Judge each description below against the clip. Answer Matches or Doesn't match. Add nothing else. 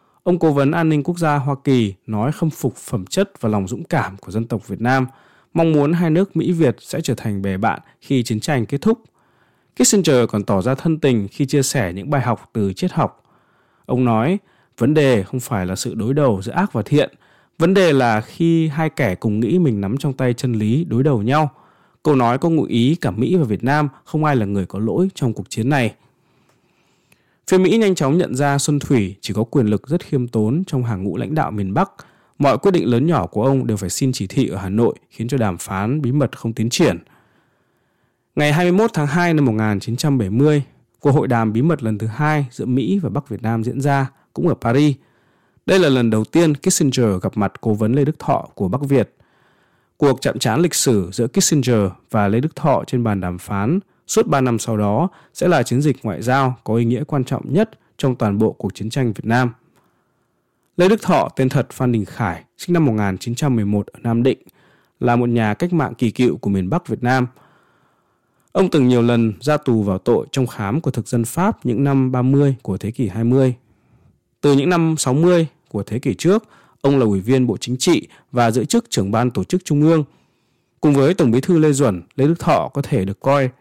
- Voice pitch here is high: Doesn't match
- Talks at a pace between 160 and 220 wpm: Doesn't match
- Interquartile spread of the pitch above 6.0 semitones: Doesn't match